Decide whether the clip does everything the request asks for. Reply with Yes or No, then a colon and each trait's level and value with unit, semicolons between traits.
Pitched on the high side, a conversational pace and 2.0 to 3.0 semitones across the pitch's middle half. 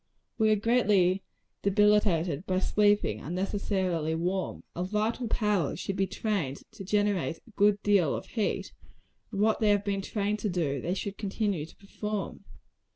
Yes: high, 200 Hz; average, 160 wpm; narrow, 2.5 semitones